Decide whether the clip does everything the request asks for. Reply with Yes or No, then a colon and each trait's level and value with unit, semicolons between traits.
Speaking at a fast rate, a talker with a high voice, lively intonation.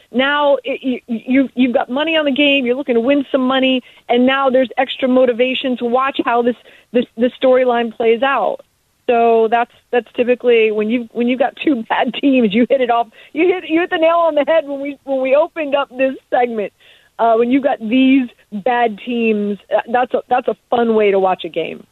No: fast, 220 wpm; very high, 255 Hz; narrow, 2.6 semitones